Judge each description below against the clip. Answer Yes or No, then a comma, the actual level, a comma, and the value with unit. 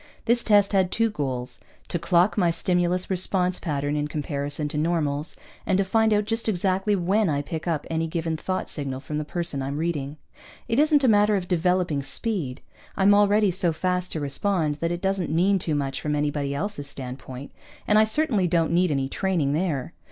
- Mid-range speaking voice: Yes, medium, 170 Hz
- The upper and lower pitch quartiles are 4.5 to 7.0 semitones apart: Yes, average, 4.9 semitones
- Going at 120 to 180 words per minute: No, average, 195 wpm